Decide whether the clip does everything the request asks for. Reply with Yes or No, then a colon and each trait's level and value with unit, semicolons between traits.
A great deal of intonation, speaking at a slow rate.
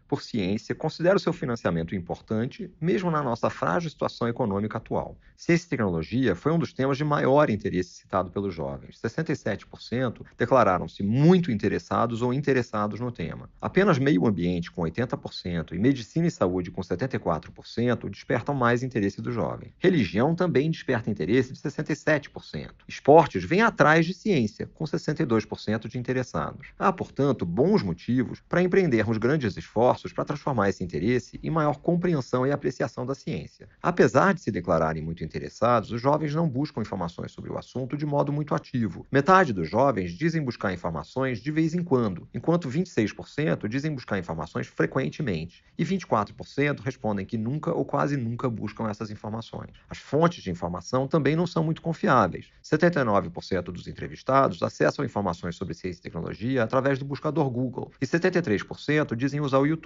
No: wide, 6.7 semitones; average, 160 wpm